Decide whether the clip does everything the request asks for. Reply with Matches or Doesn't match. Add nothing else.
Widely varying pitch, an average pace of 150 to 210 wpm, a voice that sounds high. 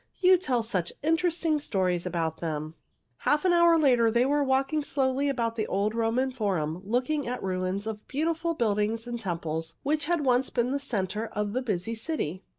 Matches